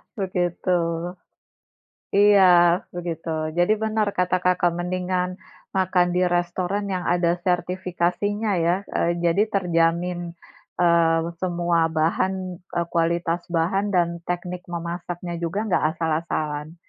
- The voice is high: No, medium, 175 Hz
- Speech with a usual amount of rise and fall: No, narrow, 1.4 semitones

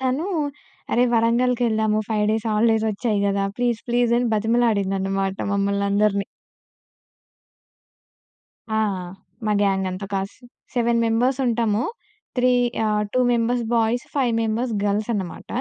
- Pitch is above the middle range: Yes, high, 220 Hz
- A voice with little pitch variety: No, average, 3.0 semitones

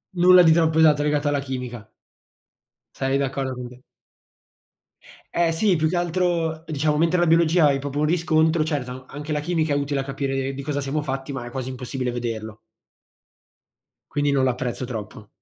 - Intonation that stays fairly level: No, average, 3.4 semitones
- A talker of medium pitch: Yes, medium, 145 Hz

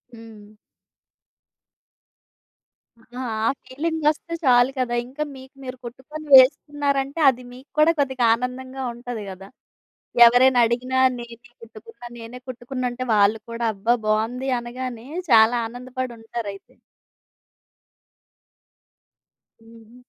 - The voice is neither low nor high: No, very high, 250 Hz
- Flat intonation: Yes, narrow, 2.2 semitones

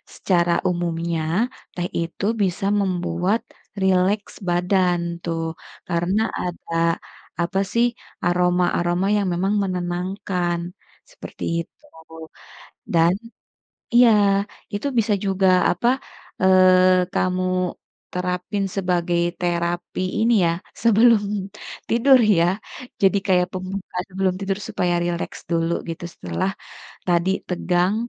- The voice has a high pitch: No, medium, 180 Hz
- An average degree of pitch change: No, narrow, 1.9 semitones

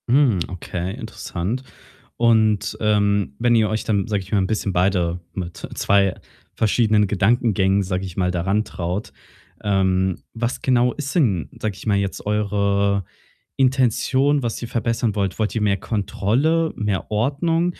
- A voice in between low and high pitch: No, low, 105 Hz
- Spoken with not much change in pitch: No, average, 3.5 semitones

